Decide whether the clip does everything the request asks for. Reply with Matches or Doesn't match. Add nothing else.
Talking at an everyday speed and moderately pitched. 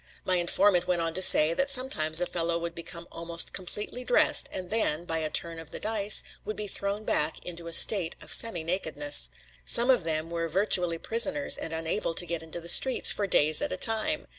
Doesn't match